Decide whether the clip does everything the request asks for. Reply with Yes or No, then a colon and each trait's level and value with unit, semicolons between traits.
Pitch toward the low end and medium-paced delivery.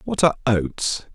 Yes: low, 130 Hz; average, 155 wpm